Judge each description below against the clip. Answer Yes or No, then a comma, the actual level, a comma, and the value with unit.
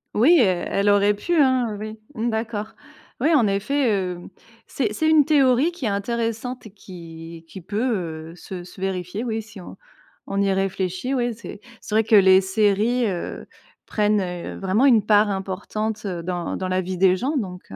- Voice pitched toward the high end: Yes, high, 205 Hz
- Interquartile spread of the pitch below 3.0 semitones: No, average, 3.8 semitones